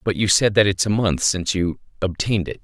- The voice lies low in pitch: Yes, very low, 95 Hz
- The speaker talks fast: Yes, fast, 250 wpm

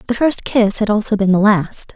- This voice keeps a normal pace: No, fast, 245 wpm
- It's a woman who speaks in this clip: Yes, female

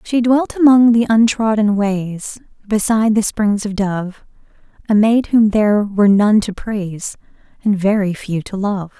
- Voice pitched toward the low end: No, high, 210 Hz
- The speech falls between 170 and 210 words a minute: No, average, 160 wpm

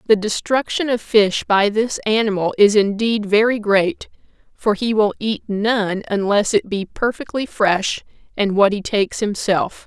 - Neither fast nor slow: Yes, average, 160 wpm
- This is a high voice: Yes, high, 215 Hz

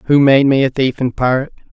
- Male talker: Yes, male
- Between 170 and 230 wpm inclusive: Yes, fast, 205 wpm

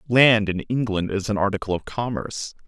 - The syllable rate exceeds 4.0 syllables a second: Yes, 5.4 syllables/s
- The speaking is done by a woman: No, male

